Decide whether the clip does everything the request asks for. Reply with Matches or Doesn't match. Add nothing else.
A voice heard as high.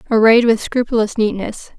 Matches